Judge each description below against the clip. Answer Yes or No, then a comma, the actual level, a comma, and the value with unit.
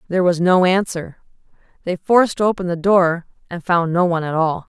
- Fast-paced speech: No, average, 190 wpm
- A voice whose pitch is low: No, medium, 175 Hz